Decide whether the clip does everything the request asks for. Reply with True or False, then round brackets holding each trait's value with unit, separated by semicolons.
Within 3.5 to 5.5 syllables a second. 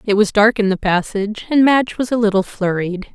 False (5.8 syllables/s)